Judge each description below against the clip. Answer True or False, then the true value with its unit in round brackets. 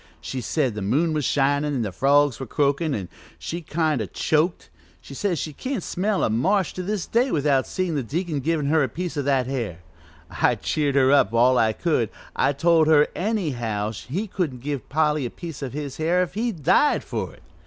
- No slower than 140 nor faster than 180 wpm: False (205 wpm)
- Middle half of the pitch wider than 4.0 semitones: True (4.7 semitones)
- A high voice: False (145 Hz)